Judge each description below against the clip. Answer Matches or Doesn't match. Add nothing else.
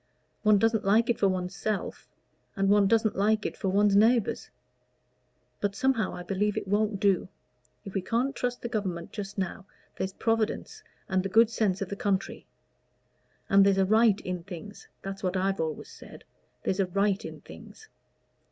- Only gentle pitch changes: Matches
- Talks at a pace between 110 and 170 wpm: Doesn't match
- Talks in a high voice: Matches